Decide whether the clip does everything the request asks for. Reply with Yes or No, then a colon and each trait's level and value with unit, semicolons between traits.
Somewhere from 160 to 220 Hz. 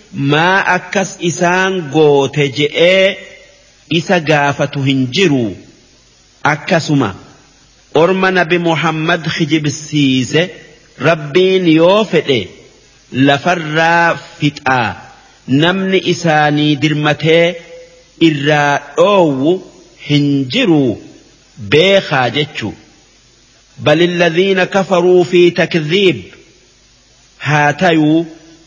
Yes: medium, 165 Hz